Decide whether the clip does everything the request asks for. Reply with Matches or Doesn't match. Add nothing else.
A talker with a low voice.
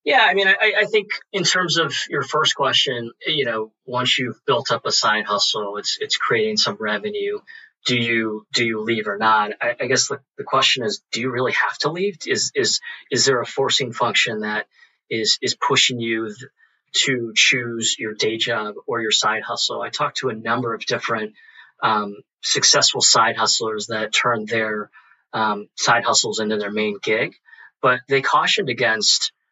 Matches